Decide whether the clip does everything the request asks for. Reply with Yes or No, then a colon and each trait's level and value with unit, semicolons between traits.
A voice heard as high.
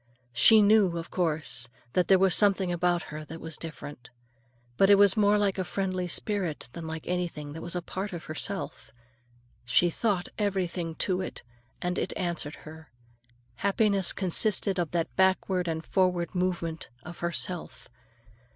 No: medium, 180 Hz